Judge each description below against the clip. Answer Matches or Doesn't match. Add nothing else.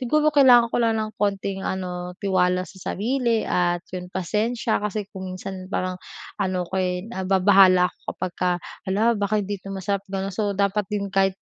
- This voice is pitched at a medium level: Doesn't match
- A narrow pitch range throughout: Matches